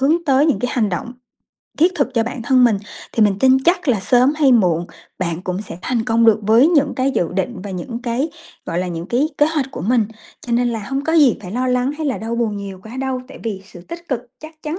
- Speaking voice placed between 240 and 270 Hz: Yes, high, 245 Hz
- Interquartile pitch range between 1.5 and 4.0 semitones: No, average, 4.9 semitones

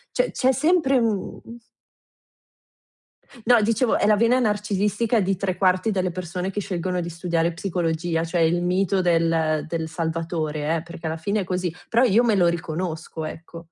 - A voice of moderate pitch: Yes, medium, 180 Hz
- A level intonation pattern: No, average, 3.8 semitones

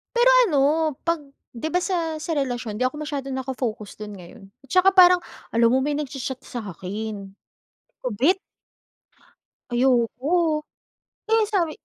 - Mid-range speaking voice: No, very high, 270 Hz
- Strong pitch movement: Yes, wide, 6.1 semitones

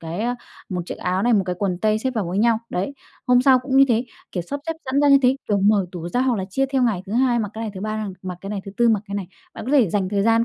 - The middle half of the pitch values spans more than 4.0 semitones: Yes, average, 4.4 semitones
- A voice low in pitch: No, high, 215 Hz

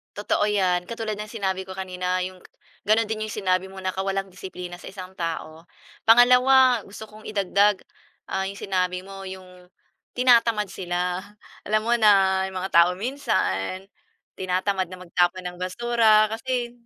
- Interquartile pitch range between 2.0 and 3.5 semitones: Yes, average, 2.8 semitones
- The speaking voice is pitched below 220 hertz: Yes, high, 190 Hz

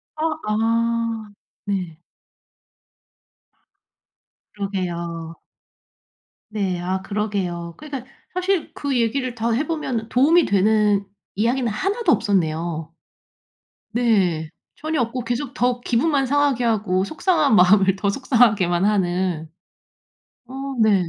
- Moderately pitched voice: No, high, 220 Hz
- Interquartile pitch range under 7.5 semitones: Yes, average, 5.3 semitones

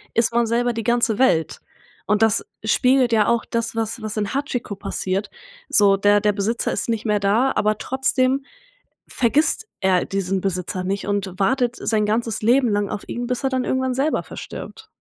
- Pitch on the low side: No, high, 225 Hz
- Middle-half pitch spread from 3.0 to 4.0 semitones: Yes, average, 3.3 semitones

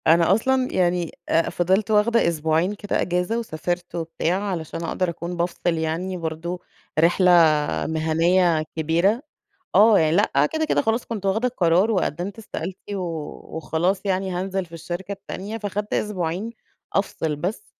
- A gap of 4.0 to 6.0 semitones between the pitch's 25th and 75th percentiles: No, average, 3.5 semitones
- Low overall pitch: No, medium, 180 Hz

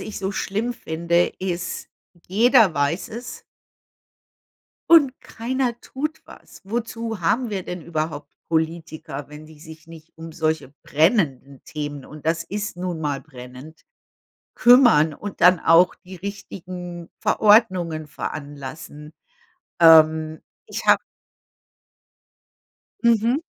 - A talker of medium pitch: Yes, medium, 170 Hz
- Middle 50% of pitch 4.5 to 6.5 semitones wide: Yes, average, 4.9 semitones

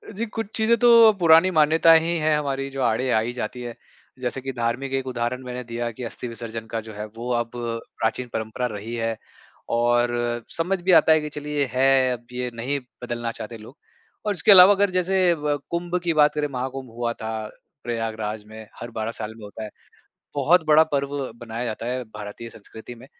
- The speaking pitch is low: Yes, low, 125 Hz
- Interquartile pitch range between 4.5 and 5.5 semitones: Yes, average, 4.8 semitones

